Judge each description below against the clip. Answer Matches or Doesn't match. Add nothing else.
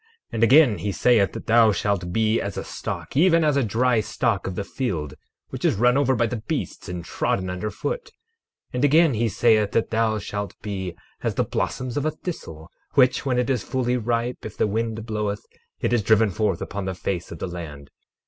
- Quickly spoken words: Matches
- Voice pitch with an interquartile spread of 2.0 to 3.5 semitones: Doesn't match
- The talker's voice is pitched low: Matches